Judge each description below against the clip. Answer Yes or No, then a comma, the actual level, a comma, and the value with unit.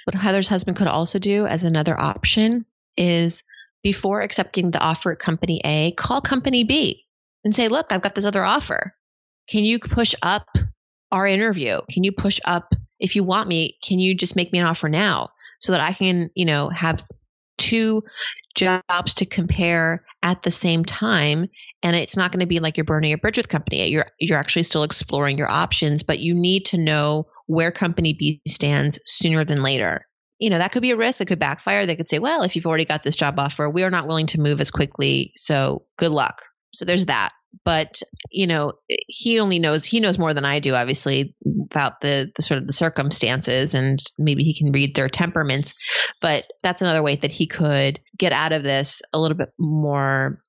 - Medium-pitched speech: Yes, medium, 165 Hz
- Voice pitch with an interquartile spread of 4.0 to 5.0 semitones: Yes, average, 4.3 semitones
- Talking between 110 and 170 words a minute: No, fast, 205 wpm